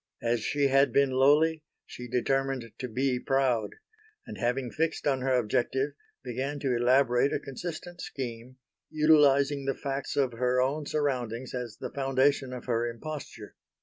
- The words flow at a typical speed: Yes, average, 150 wpm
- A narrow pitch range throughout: Yes, narrow, 2.3 semitones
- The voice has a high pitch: No, low, 135 Hz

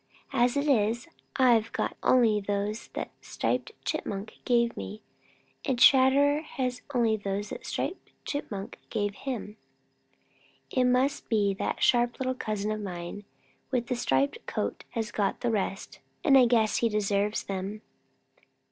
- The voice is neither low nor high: No, high, 230 Hz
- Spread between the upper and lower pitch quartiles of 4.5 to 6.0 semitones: No, average, 3.7 semitones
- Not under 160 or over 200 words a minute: No, average, 145 wpm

